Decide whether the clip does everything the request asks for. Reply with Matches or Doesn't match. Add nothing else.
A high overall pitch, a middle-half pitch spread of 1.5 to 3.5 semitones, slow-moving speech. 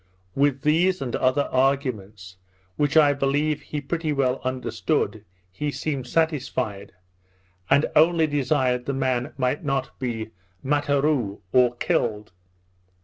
Doesn't match